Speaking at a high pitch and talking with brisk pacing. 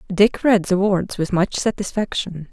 No: high, 195 Hz; average, 165 wpm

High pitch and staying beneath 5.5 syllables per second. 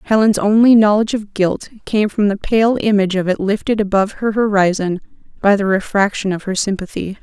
No: high, 205 Hz; 5.8 syllables/s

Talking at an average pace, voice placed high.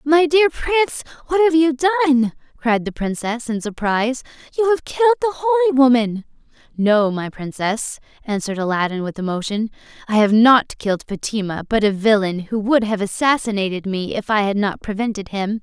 Yes: average, 170 wpm; high, 240 Hz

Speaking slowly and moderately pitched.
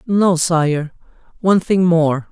Yes: slow, 130 wpm; medium, 170 Hz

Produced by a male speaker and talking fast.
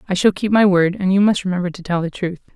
No: female; fast, 305 wpm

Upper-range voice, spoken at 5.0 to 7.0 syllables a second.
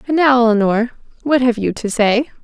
Yes: high, 240 Hz; 5.1 syllables/s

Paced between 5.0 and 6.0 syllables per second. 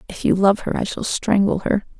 Yes: 5.4 syllables/s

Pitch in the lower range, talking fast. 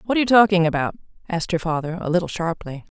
No: medium, 175 Hz; fast, 220 wpm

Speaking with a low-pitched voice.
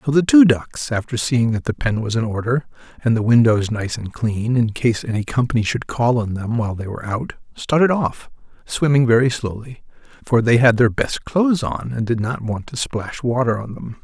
Yes: low, 120 Hz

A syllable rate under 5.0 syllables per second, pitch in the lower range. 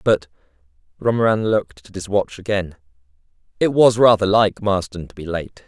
No: 5.2 syllables/s; low, 100 Hz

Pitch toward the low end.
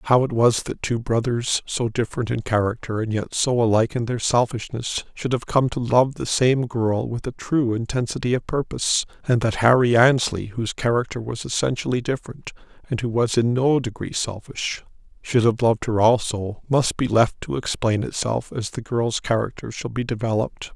Yes: low, 120 Hz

